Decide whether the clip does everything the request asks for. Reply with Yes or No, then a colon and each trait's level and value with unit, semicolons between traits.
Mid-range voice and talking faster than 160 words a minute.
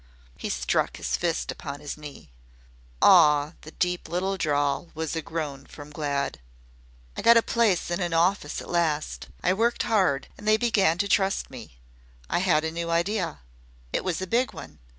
Yes: medium, 170 Hz; average, 180 wpm